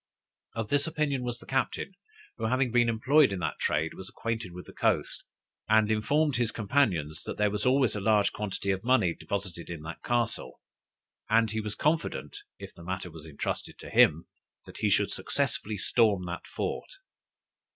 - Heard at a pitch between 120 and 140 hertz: No, low, 110 Hz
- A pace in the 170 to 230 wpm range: Yes, average, 175 wpm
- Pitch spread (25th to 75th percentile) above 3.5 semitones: Yes, average, 5.0 semitones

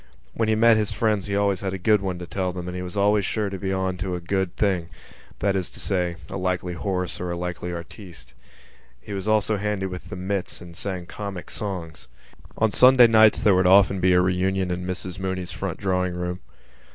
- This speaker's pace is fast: Yes, fast, 220 wpm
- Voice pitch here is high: No, very low, 95 Hz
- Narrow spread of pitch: Yes, narrow, 2.1 semitones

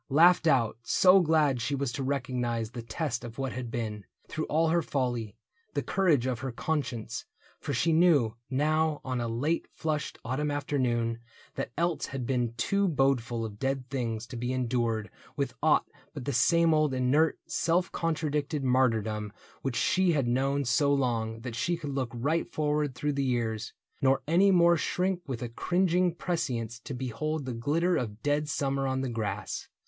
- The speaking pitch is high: No, low, 135 Hz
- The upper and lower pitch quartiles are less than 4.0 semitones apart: No, average, 4.6 semitones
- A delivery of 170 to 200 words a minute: Yes, average, 175 wpm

